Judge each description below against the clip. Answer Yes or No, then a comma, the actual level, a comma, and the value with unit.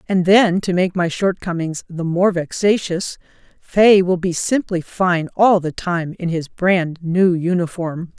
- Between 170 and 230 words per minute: No, average, 160 wpm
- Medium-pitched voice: Yes, medium, 180 Hz